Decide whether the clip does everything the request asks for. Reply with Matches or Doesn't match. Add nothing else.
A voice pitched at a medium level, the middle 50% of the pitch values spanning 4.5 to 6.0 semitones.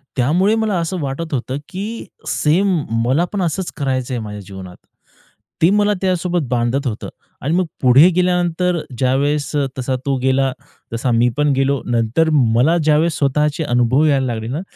Matches